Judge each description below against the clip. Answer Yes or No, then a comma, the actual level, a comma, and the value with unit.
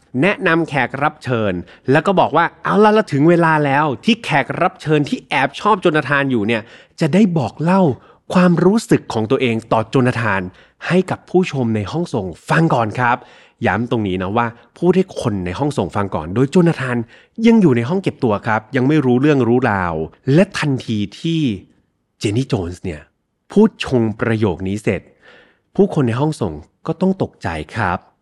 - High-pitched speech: No, low, 130 Hz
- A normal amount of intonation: No, wide, 6.7 semitones